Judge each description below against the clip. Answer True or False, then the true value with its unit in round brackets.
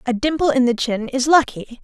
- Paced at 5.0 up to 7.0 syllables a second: True (5.3 syllables/s)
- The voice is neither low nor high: False (260 Hz)